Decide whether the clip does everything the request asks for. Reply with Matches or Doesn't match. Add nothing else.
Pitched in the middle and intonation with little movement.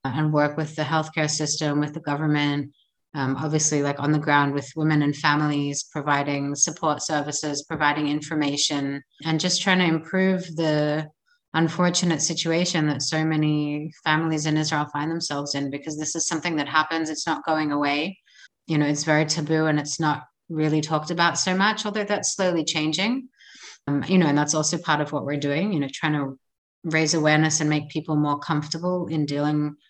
Matches